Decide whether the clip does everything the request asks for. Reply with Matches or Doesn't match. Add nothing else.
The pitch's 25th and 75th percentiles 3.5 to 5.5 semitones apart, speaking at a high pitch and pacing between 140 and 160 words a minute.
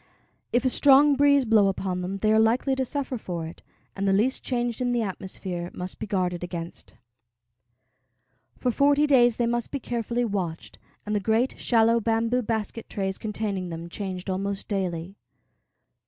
Doesn't match